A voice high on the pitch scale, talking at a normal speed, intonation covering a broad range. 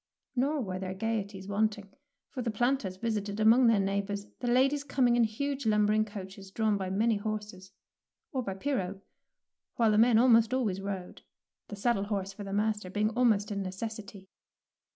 No: high, 210 Hz; average, 175 wpm; average, 2.8 semitones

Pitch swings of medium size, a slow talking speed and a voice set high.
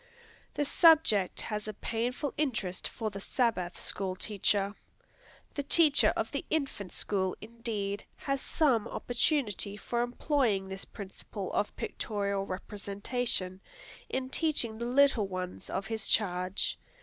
Yes: average, 4.3 semitones; slow, 125 wpm; high, 215 Hz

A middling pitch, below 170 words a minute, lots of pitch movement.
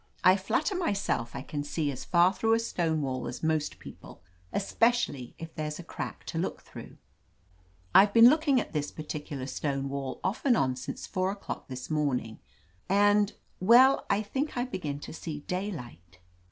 No: medium, 165 Hz; average, 180 wpm; wide, 6.6 semitones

